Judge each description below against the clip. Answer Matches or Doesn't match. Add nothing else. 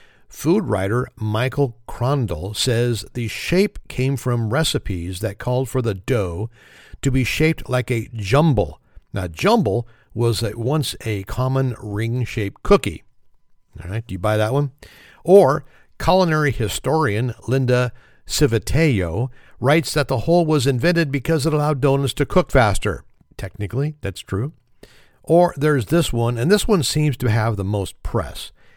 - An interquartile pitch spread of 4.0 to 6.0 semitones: Matches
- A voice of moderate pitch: Doesn't match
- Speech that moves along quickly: Doesn't match